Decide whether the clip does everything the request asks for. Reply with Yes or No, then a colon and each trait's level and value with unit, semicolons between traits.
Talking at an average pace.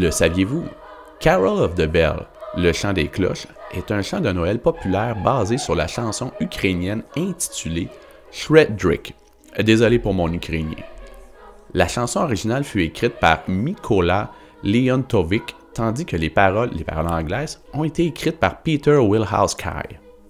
No: slow, 140 wpm